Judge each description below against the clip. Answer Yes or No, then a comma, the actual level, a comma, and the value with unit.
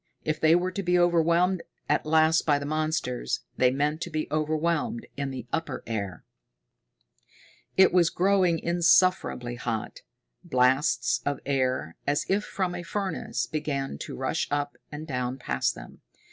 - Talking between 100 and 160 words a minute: Yes, average, 150 wpm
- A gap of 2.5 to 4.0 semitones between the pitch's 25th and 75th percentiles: No, average, 4.7 semitones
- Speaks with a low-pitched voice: No, medium, 155 Hz